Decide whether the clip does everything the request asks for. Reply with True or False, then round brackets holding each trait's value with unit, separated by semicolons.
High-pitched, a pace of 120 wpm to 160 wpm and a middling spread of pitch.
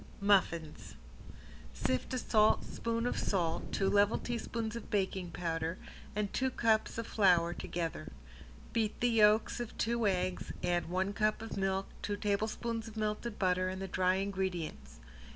True (200 Hz; 150 wpm; 3.2 semitones)